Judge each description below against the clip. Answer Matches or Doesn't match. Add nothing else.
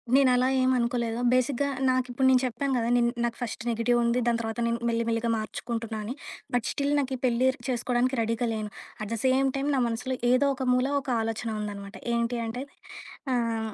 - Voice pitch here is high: Matches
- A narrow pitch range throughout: Matches